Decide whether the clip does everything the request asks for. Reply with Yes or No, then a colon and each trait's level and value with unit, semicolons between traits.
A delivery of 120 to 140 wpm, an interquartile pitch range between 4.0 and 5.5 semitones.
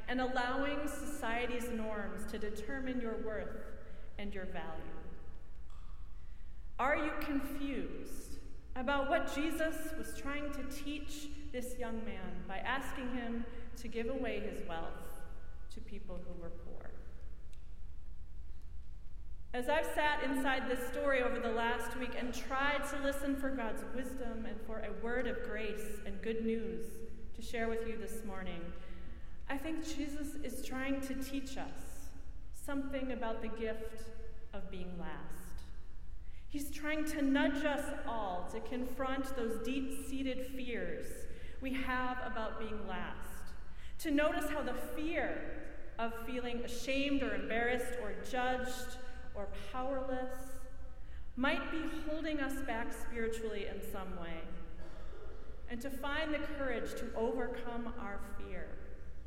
Yes: slow, 135 wpm; average, 4.7 semitones